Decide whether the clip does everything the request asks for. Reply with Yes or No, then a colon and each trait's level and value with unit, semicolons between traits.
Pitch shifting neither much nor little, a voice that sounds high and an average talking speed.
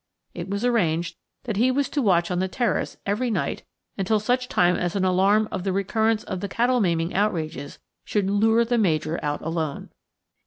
Yes: average, 4.3 semitones; high, 200 Hz; average, 190 wpm